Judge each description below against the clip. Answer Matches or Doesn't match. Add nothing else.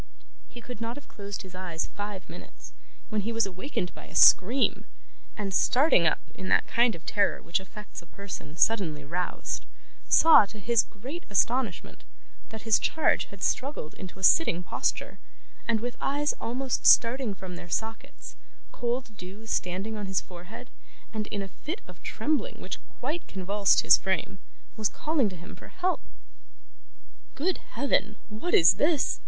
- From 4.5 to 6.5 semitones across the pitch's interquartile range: Matches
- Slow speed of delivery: Doesn't match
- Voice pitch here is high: Matches